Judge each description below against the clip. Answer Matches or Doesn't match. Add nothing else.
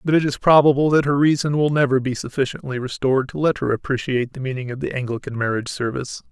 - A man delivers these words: Matches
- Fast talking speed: Matches